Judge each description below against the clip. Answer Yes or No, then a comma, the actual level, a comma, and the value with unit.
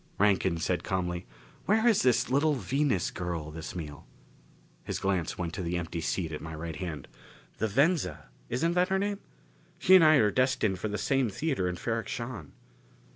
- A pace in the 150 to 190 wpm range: Yes, average, 180 wpm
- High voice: No, low, 100 Hz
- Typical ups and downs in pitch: No, wide, 8.2 semitones